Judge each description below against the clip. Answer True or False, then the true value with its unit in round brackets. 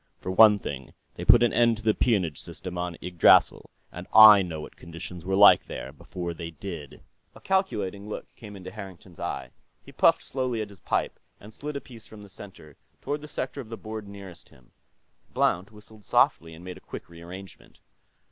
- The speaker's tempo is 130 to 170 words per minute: False (200 wpm)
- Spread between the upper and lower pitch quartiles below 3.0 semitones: False (3.9 semitones)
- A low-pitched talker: True (100 Hz)